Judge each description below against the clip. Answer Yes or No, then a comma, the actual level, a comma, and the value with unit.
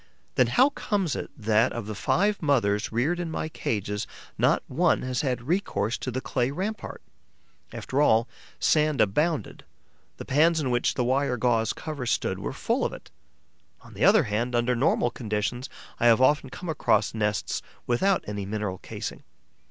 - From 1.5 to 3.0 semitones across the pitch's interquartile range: No, wide, 5.5 semitones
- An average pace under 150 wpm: No, average, 170 wpm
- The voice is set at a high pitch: No, low, 125 Hz